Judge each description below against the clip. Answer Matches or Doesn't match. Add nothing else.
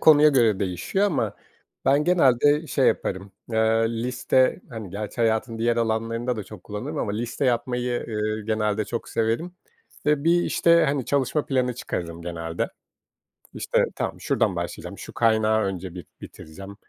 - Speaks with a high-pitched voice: Doesn't match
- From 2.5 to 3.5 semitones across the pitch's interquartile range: Doesn't match